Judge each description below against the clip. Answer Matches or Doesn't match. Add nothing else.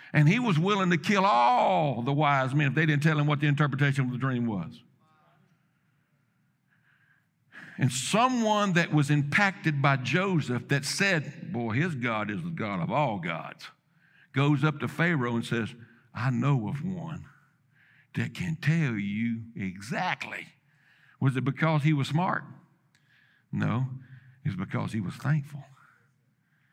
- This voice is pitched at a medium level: Matches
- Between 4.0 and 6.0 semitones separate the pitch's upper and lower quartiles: Doesn't match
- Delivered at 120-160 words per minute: Matches